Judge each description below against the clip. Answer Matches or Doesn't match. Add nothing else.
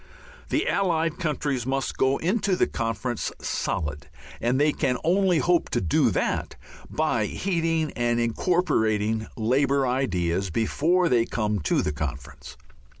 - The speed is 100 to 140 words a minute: Matches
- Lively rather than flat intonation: Matches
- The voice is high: Doesn't match